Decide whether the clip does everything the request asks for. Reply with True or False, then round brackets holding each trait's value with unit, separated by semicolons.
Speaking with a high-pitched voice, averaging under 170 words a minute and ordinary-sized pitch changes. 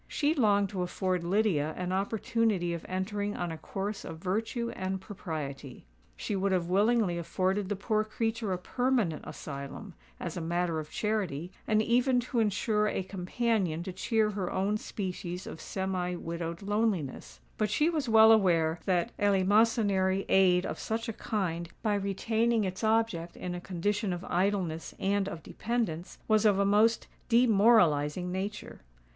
True (195 Hz; 160 wpm; 3.6 semitones)